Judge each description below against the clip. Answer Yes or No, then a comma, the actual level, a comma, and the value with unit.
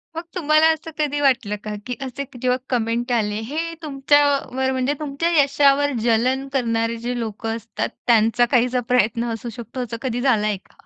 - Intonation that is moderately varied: Yes, average, 3.3 semitones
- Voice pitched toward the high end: Yes, very high, 250 Hz